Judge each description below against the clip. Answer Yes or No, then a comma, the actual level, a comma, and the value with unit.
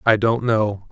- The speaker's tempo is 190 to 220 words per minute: Yes, average, 200 wpm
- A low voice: Yes, low, 110 Hz